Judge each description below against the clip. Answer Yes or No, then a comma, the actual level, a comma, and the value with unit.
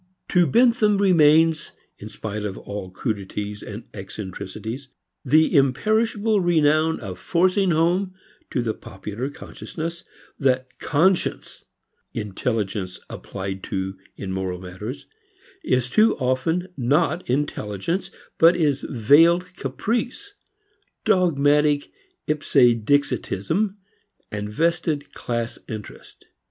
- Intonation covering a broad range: Yes, wide, 8.2 semitones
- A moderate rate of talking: No, slow, 95 wpm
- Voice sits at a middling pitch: Yes, medium, 145 Hz